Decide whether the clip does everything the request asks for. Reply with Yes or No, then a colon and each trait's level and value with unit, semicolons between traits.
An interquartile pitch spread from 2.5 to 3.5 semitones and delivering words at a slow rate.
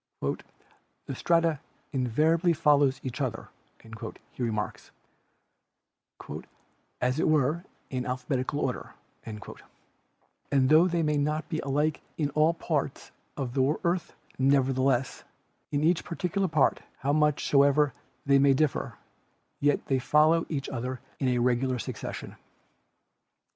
Yes: average, 3.1 semitones; slow, 120 wpm